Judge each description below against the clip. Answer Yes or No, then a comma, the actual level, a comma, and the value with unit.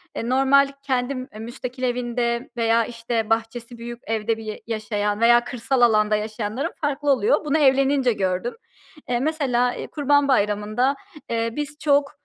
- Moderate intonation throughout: Yes, average, 3.3 semitones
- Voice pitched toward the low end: No, high, 240 Hz